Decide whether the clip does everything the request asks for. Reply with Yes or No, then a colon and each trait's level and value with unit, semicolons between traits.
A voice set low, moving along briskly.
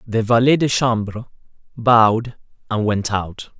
No: low, 115 Hz; slow, 135 wpm